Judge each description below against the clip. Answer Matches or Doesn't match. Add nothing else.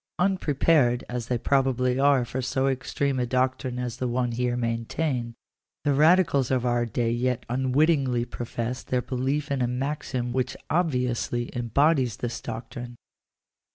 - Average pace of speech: Matches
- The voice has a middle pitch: Doesn't match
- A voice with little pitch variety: Matches